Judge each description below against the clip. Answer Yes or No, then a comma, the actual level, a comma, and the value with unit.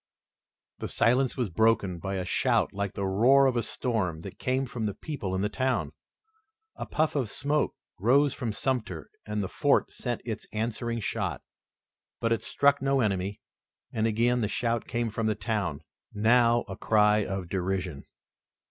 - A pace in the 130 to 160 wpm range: No, average, 170 wpm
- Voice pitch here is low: Yes, low, 110 Hz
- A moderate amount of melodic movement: Yes, average, 4.0 semitones